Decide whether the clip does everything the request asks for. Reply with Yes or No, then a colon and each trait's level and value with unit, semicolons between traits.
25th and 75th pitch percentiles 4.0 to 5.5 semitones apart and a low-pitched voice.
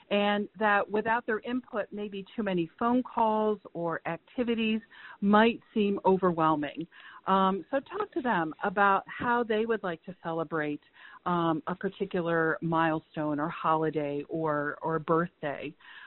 No: average, 4.9 semitones; medium, 185 Hz